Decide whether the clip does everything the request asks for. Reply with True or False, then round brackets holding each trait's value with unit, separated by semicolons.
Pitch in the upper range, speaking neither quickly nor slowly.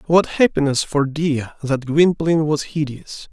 False (150 Hz; 145 wpm)